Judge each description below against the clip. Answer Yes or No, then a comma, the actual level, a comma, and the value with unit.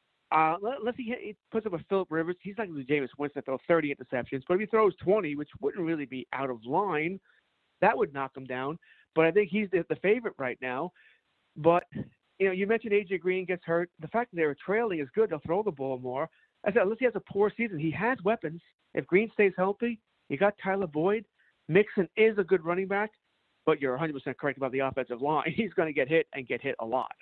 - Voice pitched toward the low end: No, medium, 175 Hz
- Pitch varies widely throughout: Yes, wide, 6.2 semitones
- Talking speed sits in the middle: No, fast, 235 wpm